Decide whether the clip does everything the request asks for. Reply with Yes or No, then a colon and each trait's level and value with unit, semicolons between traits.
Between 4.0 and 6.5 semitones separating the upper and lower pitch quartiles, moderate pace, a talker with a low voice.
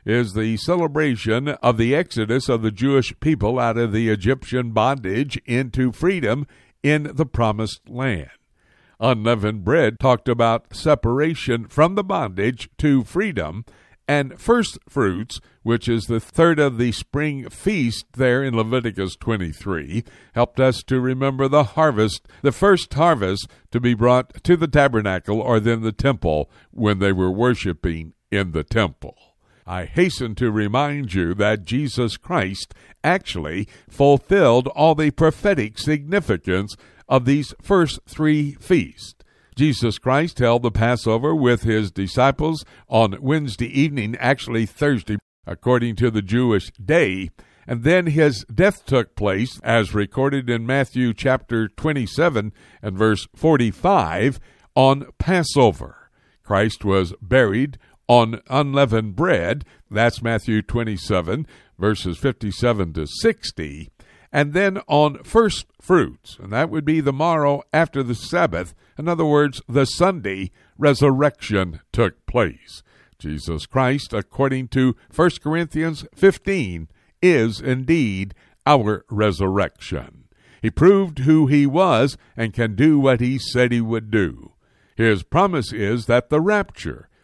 No: average, 5.2 semitones; slow, 130 wpm; low, 120 Hz